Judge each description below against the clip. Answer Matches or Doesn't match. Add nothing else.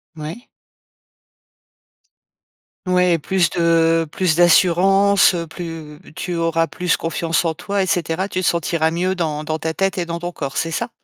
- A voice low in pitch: Doesn't match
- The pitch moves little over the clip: Matches